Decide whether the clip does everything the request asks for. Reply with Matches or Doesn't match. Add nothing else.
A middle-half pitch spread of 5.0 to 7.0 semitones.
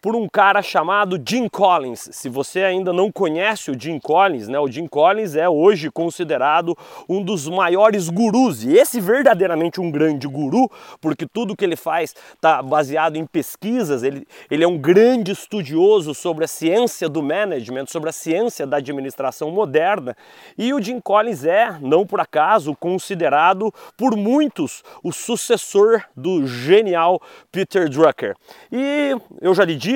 Matches